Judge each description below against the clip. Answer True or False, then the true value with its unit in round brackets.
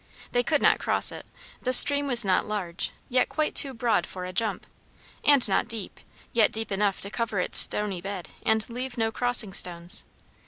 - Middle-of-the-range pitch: False (220 Hz)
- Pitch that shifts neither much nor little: True (4.0 semitones)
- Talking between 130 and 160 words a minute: False (190 wpm)